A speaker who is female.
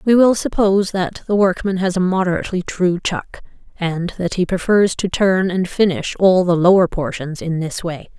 Yes: female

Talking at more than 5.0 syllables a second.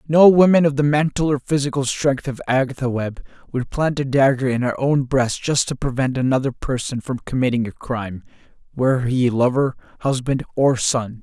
Yes: 5.2 syllables/s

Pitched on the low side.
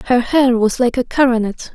No: high, 245 Hz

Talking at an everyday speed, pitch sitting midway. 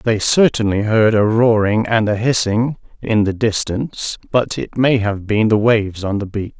No: average, 190 wpm; low, 110 Hz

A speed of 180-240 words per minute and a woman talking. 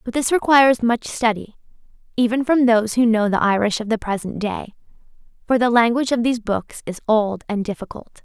Yes: average, 190 wpm; female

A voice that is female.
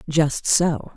Yes: female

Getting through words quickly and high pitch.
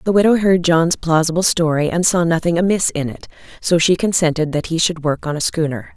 No: fast, 220 wpm; medium, 165 Hz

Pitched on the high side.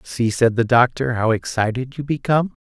No: low, 125 Hz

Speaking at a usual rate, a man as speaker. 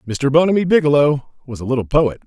Yes: average, 185 wpm; male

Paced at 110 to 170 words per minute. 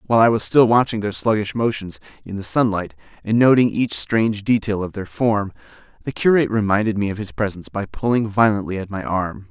No: average, 200 wpm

